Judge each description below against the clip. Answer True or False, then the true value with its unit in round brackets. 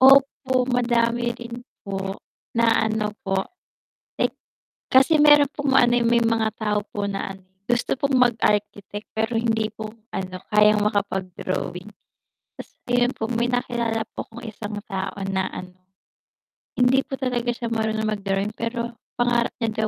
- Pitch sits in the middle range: False (225 Hz)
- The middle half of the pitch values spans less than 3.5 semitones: True (2.7 semitones)